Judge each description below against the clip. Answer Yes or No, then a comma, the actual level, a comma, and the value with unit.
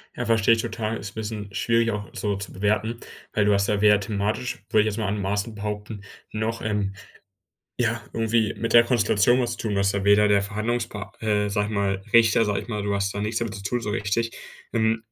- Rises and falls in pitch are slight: Yes, narrow, 1.9 semitones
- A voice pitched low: Yes, low, 105 Hz